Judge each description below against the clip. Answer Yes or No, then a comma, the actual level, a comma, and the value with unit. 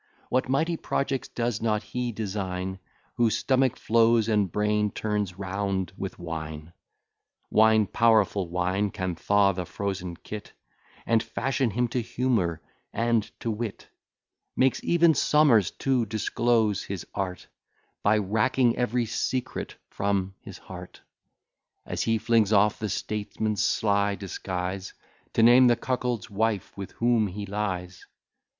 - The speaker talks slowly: Yes, slow, 130 wpm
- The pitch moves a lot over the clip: No, average, 3.3 semitones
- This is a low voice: Yes, low, 105 Hz